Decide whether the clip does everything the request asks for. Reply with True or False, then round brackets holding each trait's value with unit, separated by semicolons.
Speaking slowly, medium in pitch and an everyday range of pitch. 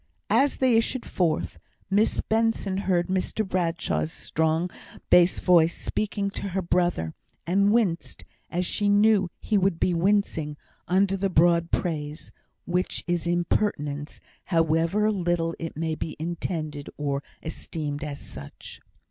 True (130 wpm; 175 Hz; 3.6 semitones)